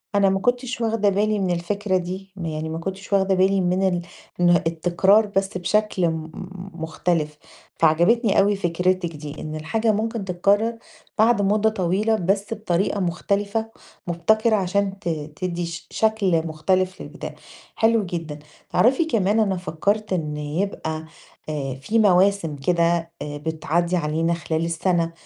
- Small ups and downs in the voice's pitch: No, average, 3.6 semitones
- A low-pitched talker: No, medium, 185 Hz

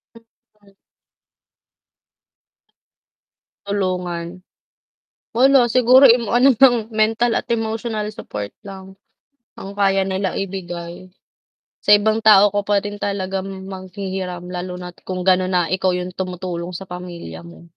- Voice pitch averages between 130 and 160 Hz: No, high, 190 Hz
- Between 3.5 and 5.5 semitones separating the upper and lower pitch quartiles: No, average, 2.8 semitones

